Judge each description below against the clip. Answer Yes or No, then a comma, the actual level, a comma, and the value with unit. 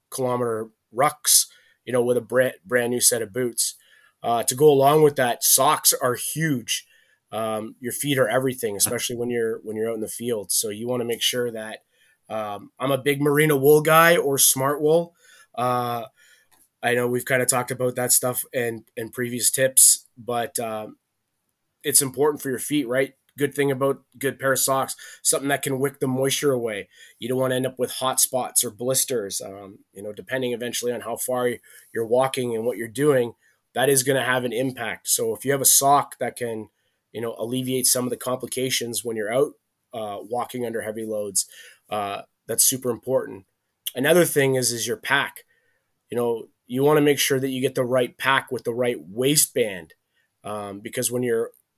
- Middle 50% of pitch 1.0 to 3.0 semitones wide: Yes, narrow, 2.6 semitones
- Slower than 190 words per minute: No, average, 200 wpm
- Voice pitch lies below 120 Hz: No, low, 125 Hz